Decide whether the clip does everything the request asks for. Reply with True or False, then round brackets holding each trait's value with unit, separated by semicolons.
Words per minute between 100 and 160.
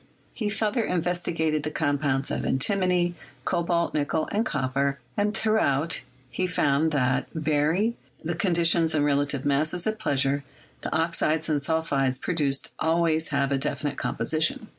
True (140 wpm)